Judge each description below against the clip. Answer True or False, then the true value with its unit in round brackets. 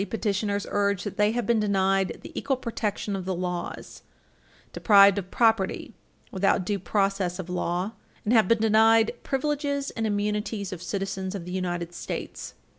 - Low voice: False (200 Hz)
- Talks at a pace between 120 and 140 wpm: False (165 wpm)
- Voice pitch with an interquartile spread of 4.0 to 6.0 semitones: False (2.8 semitones)